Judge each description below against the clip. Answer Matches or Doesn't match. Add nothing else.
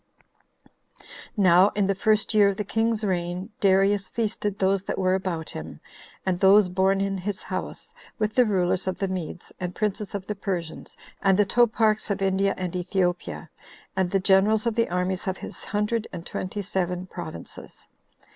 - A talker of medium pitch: Doesn't match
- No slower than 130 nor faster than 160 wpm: Doesn't match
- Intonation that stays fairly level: Matches